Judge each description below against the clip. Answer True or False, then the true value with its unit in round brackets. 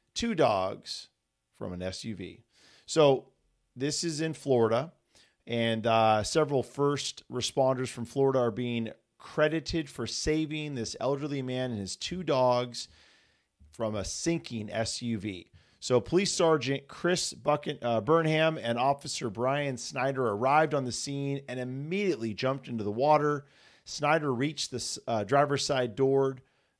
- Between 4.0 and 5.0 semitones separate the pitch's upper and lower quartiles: True (4.3 semitones)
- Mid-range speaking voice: False (130 Hz)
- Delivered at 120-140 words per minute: True (135 wpm)